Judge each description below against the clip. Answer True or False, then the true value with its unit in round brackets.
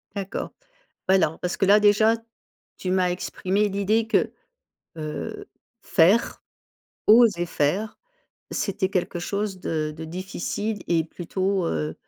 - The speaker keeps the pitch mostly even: False (3.2 semitones)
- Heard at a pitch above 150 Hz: True (190 Hz)